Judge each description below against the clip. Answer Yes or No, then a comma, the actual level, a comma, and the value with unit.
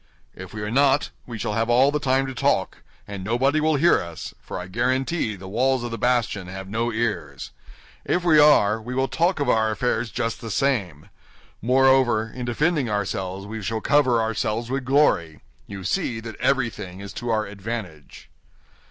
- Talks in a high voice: No, low, 115 Hz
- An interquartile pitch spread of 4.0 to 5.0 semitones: Yes, average, 4.6 semitones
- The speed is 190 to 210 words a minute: No, average, 180 wpm